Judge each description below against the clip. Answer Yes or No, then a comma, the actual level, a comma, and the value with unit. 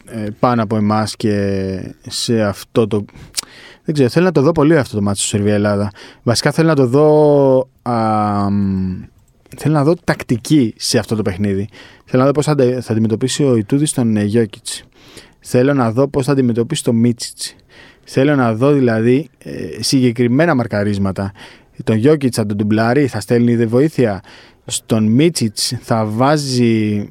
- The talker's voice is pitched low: Yes, low, 120 Hz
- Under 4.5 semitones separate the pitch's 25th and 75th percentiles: Yes, average, 4.1 semitones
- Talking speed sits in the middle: Yes, average, 155 wpm